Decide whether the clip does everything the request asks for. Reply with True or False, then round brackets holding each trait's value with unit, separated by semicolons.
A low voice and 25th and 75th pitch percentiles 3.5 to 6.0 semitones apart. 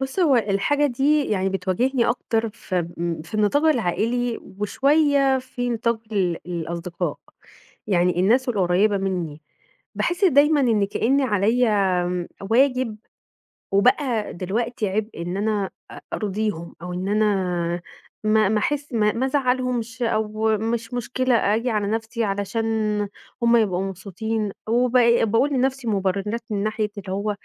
False (220 Hz; 4.1 semitones)